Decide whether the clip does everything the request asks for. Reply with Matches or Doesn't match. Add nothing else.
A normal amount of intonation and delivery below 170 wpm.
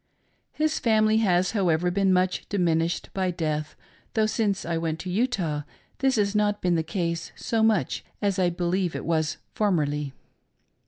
Matches